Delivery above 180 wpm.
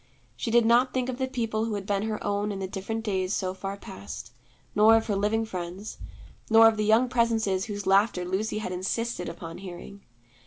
Yes: fast, 205 wpm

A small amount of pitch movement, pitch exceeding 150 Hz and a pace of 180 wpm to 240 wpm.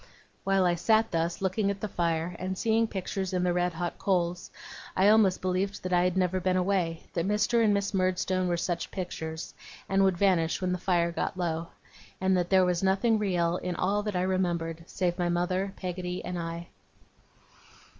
Yes: narrow, 1.8 semitones; medium, 185 Hz; average, 195 wpm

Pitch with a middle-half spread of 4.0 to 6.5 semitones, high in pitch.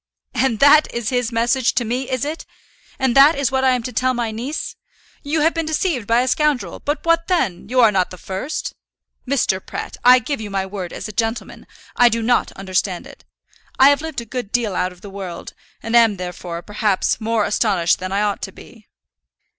Yes: average, 4.7 semitones; high, 235 Hz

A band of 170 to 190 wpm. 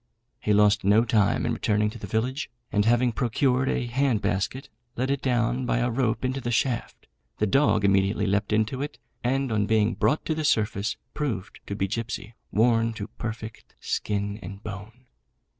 Yes: average, 180 wpm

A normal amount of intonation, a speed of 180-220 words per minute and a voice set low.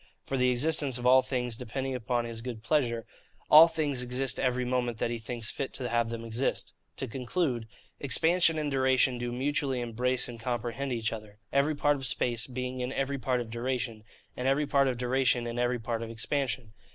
No: narrow, 2.3 semitones; average, 200 wpm; low, 125 Hz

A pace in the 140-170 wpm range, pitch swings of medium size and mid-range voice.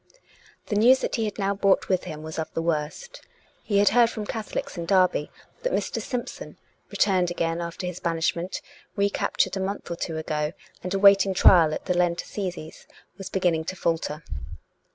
No: average, 180 wpm; average, 3.3 semitones; medium, 180 Hz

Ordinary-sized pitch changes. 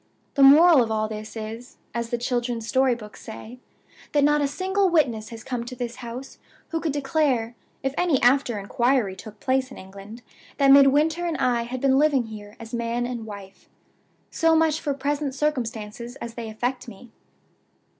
Yes: average, 3.7 semitones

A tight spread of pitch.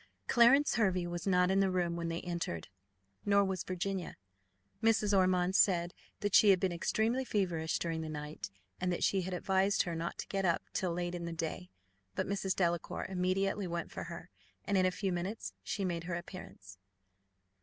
Yes: narrow, 2.3 semitones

